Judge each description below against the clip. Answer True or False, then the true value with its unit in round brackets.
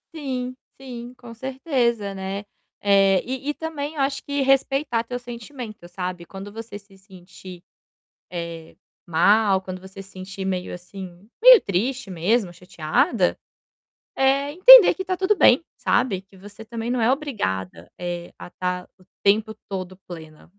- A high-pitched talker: True (205 Hz)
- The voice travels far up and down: True (5.9 semitones)